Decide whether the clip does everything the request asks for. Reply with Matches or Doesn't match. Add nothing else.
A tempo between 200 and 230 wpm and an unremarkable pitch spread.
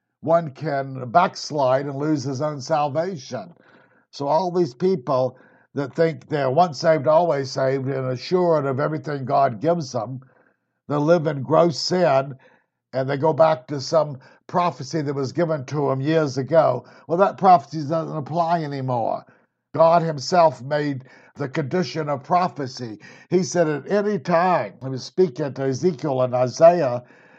Doesn't match